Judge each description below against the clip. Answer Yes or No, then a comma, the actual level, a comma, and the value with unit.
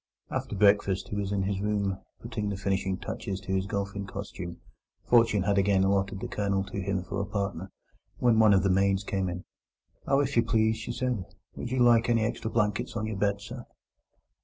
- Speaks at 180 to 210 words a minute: Yes, average, 195 wpm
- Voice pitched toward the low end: Yes, low, 100 Hz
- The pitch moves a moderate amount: No, narrow, 2.2 semitones